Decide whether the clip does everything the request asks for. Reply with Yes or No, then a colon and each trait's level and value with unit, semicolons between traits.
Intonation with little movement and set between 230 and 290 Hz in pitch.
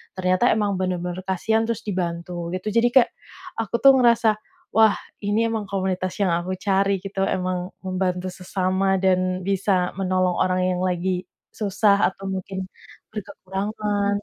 No: narrow, 2.0 semitones; high, 190 Hz